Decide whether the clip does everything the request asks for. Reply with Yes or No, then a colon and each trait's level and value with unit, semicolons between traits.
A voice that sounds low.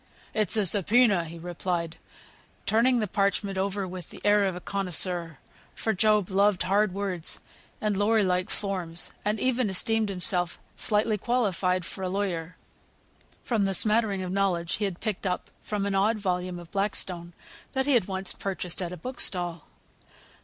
No: high, 195 Hz